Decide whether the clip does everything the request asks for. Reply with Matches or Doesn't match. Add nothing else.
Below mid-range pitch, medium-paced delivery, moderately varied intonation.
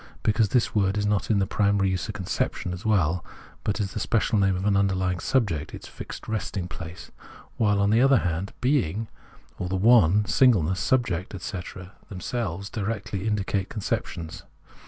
Matches